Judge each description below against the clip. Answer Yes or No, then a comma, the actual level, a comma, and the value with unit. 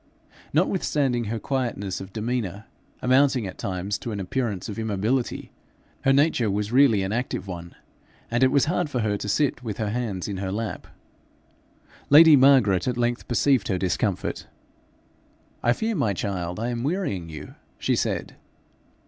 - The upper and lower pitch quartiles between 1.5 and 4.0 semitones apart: No, average, 5.0 semitones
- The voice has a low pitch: Yes, low, 115 Hz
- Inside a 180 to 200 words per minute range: No, average, 160 wpm